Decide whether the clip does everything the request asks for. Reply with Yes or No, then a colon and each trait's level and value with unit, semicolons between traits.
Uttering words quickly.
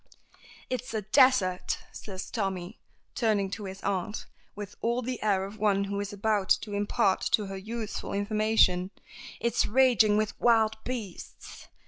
No: average, 145 wpm